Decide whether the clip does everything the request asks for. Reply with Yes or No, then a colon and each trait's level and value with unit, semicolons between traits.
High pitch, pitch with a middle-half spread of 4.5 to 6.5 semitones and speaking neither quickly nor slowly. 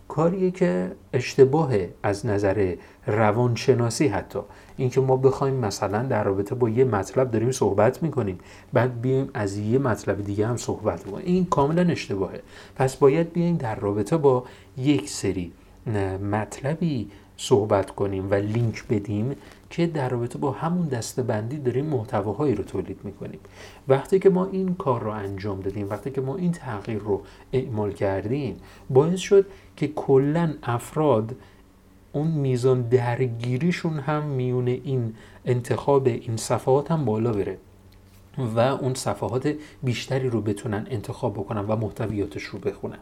No: low, 125 Hz; average, 5.0 semitones; average, 140 wpm